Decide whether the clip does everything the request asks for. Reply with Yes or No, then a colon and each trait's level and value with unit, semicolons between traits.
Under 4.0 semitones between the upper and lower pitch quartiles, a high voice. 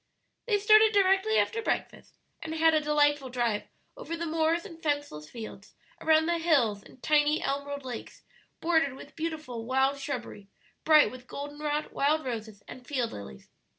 No: average, 4.4 semitones; very high, 290 Hz